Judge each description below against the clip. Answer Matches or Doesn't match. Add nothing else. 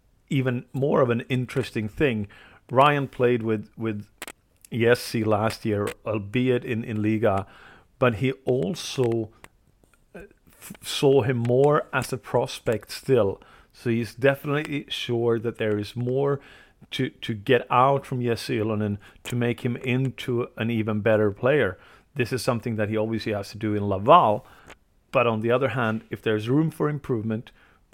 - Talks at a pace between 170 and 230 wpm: Doesn't match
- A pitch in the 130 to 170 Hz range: Doesn't match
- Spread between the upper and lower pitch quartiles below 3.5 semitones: Matches